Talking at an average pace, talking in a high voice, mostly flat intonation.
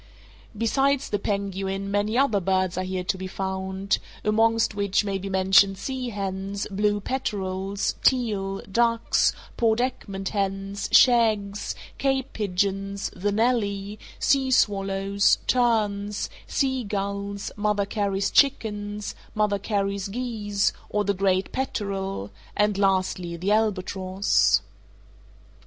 No: slow, 115 wpm; high, 200 Hz; narrow, 1.8 semitones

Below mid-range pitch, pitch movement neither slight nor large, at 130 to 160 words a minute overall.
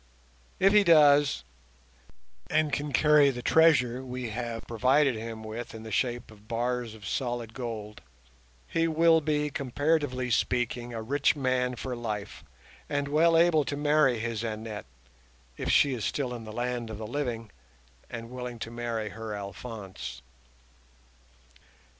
Yes: low, 125 Hz; average, 4.2 semitones; average, 145 wpm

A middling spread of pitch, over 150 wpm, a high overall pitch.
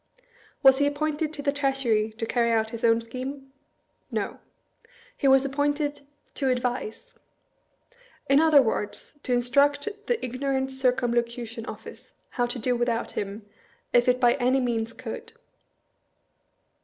No: average, 3.2 semitones; average, 140 wpm; very high, 255 Hz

